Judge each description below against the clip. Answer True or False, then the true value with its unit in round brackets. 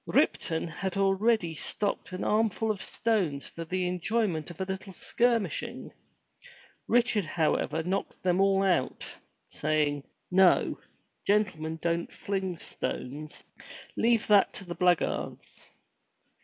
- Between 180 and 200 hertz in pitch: True (185 Hz)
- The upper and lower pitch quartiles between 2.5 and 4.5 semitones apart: True (3.6 semitones)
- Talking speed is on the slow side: True (120 wpm)